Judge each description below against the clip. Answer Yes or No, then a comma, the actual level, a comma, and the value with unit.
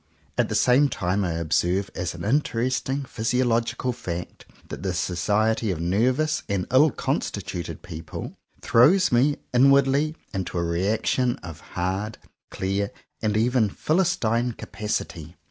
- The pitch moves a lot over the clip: Yes, wide, 6.0 semitones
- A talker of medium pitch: No, low, 110 Hz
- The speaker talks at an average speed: No, slow, 130 wpm